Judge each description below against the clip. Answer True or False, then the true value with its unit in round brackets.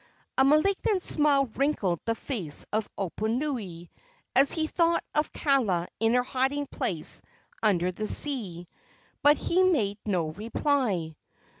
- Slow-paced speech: True (130 wpm)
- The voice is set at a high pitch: True (245 Hz)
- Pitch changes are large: True (7.0 semitones)